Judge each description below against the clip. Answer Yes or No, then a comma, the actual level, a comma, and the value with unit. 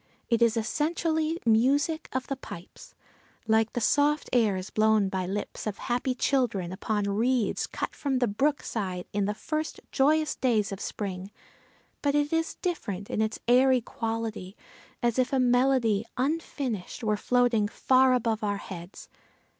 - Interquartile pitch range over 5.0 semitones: No, average, 4.5 semitones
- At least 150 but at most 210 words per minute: Yes, average, 155 wpm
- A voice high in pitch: Yes, high, 235 Hz